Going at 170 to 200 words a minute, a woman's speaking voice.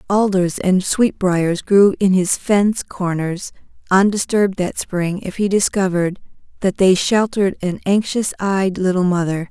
No: average, 140 wpm; female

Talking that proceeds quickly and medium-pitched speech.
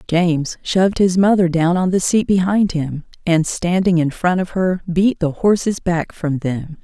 No: average, 195 wpm; medium, 175 Hz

